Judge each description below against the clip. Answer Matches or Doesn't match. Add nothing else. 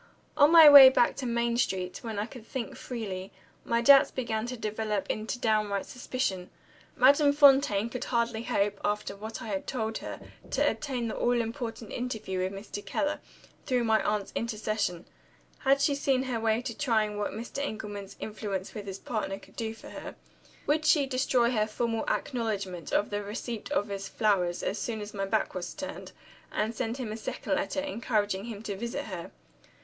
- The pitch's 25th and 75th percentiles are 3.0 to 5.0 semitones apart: Matches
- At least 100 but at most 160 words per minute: Doesn't match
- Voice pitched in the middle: Doesn't match